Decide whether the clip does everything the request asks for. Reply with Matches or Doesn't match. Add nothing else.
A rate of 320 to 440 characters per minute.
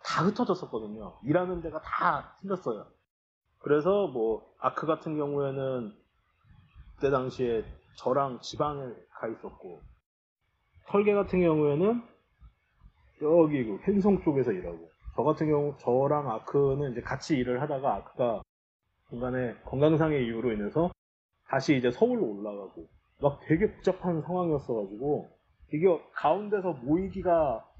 Doesn't match